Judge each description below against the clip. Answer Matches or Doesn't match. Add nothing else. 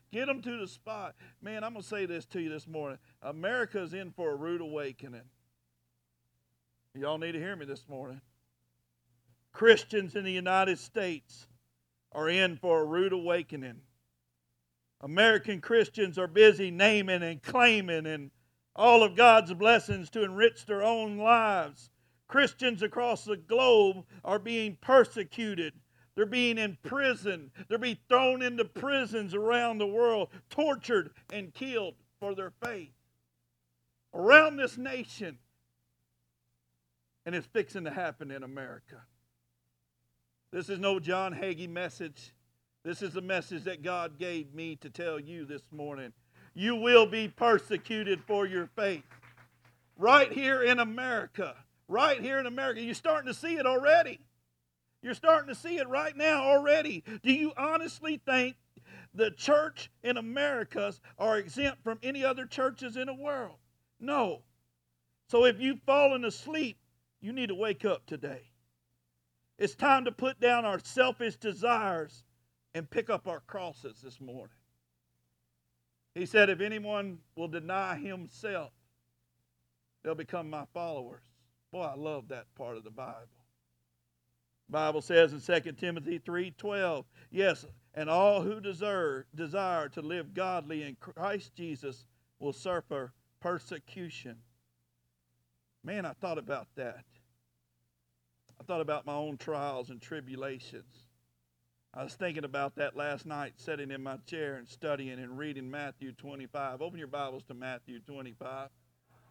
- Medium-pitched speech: Matches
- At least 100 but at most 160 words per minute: Matches